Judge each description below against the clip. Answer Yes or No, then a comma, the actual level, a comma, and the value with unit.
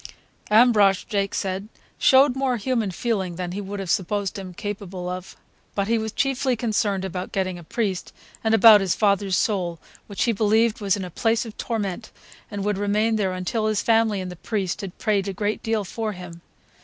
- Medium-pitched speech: No, high, 205 Hz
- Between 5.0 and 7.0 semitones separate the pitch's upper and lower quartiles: No, average, 2.8 semitones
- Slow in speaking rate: No, average, 195 wpm